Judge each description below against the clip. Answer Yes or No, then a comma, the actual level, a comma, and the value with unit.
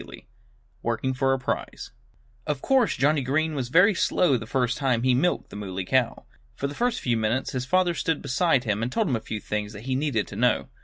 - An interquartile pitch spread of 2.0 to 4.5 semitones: No, average, 4.9 semitones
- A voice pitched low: Yes, low, 130 Hz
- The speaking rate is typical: No, fast, 220 wpm